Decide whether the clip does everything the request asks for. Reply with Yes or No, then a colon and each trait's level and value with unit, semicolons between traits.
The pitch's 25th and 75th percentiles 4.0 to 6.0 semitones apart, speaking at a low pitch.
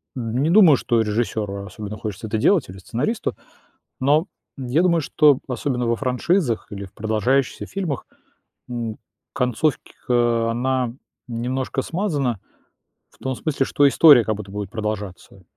Yes: average, 4.4 semitones; low, 120 Hz